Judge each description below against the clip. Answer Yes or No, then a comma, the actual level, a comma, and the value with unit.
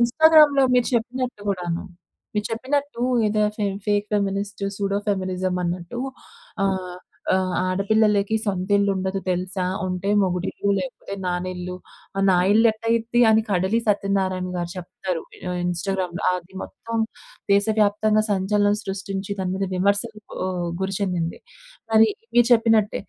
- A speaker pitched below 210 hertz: Yes, high, 200 Hz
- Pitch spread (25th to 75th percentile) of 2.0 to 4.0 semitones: Yes, average, 2.9 semitones